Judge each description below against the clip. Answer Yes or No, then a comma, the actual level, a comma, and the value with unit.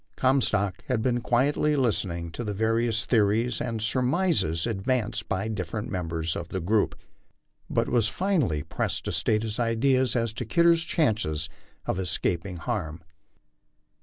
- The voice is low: Yes, low, 110 Hz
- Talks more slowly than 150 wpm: Yes, average, 140 wpm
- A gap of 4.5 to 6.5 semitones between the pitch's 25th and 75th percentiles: Yes, average, 5.2 semitones